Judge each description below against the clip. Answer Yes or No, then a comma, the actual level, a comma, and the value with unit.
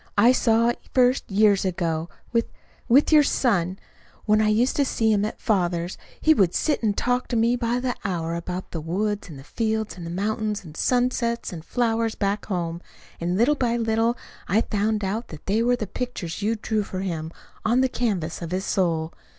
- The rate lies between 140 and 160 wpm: No, average, 200 wpm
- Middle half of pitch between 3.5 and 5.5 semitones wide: Yes, average, 4.7 semitones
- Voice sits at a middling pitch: No, high, 215 Hz